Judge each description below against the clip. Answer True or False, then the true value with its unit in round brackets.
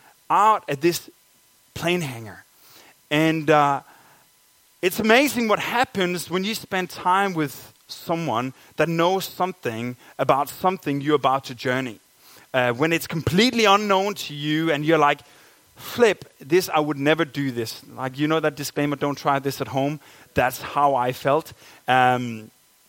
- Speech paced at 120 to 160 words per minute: True (150 wpm)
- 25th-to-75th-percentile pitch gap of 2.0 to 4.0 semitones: False (4.8 semitones)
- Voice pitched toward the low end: False (150 Hz)